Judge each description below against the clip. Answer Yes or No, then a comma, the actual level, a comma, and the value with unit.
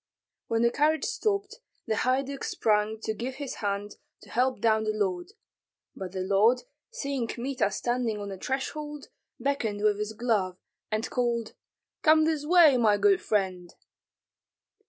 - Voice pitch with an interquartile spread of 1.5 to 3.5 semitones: No, average, 4.9 semitones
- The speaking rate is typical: Yes, average, 150 wpm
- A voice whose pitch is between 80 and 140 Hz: No, high, 230 Hz